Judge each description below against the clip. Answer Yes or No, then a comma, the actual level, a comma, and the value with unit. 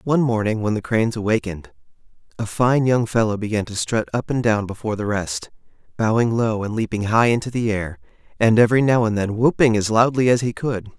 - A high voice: No, low, 110 Hz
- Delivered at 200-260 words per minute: Yes, fast, 205 wpm